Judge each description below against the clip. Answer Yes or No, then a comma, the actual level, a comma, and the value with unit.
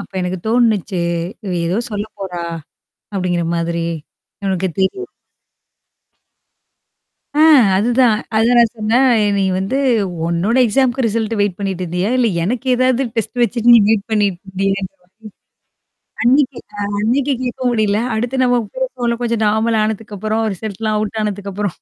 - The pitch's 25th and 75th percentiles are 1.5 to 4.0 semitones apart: Yes, average, 3.7 semitones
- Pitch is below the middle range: No, high, 215 Hz